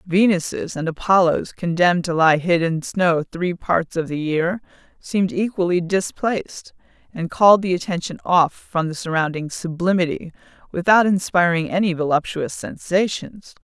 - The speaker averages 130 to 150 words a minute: Yes, slow, 135 wpm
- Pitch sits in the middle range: Yes, medium, 175 Hz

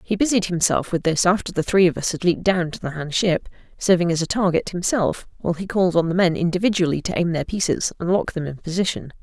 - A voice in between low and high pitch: Yes, medium, 180 Hz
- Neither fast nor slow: No, fast, 240 wpm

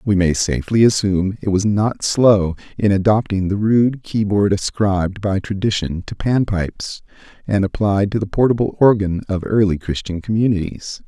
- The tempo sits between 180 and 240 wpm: No, average, 155 wpm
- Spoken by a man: Yes, male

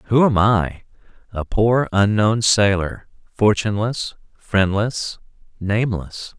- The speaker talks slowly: Yes, slow, 95 wpm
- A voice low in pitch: Yes, low, 105 Hz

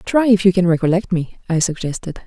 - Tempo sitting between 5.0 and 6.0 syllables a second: Yes, 5.9 syllables/s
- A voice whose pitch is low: No, medium, 185 Hz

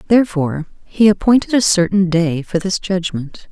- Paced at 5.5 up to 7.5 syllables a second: No, 5.1 syllables/s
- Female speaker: Yes, female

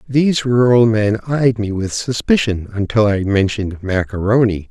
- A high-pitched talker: No, low, 110 Hz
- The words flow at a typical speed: Yes, average, 155 wpm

